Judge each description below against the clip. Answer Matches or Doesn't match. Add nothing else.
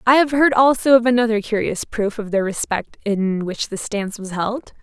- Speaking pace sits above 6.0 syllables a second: Doesn't match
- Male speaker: Doesn't match